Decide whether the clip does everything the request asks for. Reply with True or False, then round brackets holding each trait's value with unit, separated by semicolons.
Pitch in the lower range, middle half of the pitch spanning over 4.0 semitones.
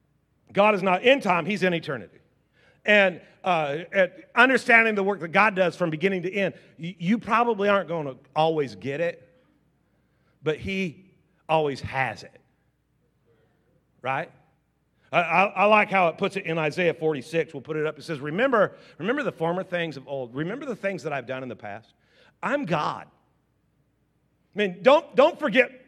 False (175 Hz; 5.0 semitones)